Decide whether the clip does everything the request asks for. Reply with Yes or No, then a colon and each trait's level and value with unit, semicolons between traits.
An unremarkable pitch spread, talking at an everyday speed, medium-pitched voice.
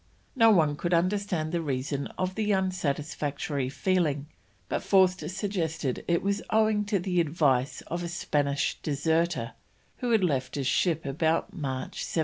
Yes: average, 4.6 semitones; average, 155 wpm; medium, 165 Hz